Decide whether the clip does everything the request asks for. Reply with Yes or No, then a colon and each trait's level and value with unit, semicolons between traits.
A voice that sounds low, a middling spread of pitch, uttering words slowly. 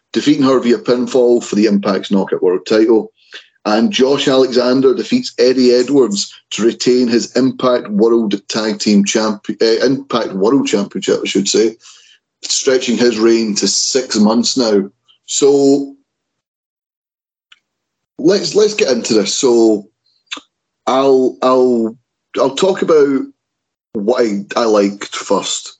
Yes: low, 125 Hz; average, 3.6 semitones; slow, 130 wpm